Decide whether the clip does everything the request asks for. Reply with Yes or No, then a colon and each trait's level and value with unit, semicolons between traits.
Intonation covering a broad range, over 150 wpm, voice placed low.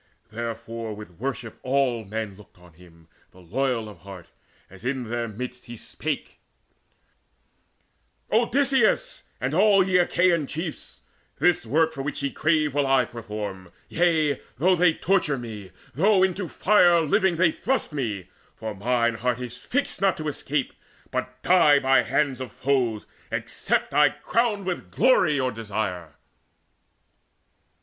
No: wide, 7.4 semitones; average, 140 wpm; low, 130 Hz